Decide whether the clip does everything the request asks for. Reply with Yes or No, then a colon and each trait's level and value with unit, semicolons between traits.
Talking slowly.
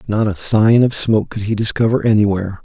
No: fast, 205 wpm